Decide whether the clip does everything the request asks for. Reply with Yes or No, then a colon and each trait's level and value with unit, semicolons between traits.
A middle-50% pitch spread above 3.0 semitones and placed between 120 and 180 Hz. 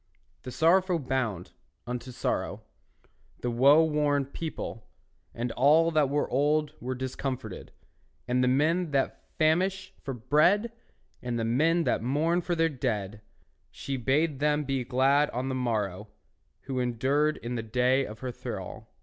Yes: average, 3.9 semitones; low, 135 Hz